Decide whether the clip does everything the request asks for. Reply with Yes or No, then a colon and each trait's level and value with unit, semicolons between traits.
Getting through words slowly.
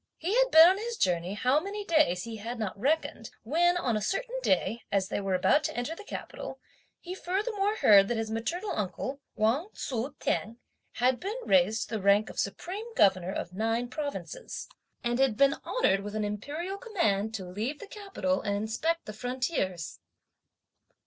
No: average, 180 wpm